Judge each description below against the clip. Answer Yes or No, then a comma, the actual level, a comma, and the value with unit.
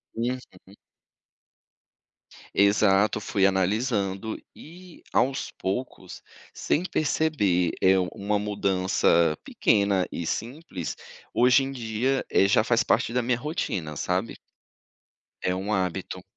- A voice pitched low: Yes, low, 105 Hz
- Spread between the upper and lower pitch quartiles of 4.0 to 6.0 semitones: Yes, average, 4.8 semitones